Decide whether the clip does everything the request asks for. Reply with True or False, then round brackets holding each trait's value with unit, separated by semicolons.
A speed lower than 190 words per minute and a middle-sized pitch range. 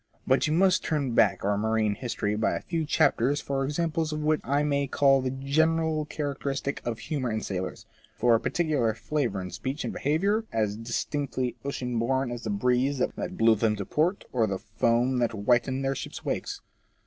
False (195 wpm; 4.6 semitones)